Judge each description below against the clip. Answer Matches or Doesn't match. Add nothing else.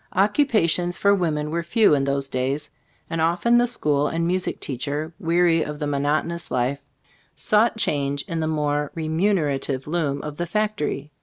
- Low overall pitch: Doesn't match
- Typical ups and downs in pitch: Matches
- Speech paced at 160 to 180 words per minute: Matches